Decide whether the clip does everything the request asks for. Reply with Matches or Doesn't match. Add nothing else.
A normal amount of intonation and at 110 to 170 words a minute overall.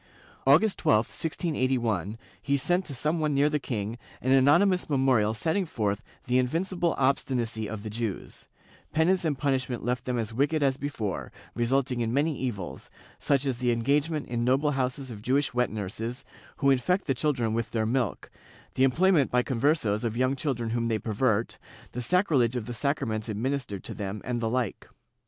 Doesn't match